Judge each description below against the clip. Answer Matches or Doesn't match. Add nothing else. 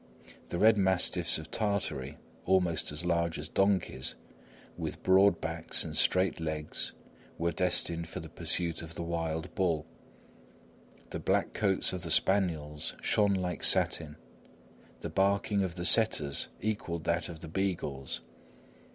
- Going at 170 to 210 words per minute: Doesn't match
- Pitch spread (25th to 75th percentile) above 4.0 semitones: Doesn't match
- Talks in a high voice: Doesn't match